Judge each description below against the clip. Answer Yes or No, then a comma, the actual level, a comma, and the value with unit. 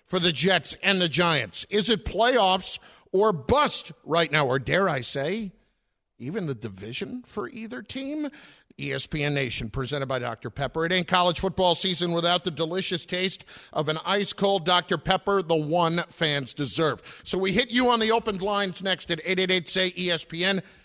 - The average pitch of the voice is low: No, medium, 180 Hz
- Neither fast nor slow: Yes, average, 180 wpm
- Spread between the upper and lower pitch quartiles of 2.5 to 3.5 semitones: No, average, 4.0 semitones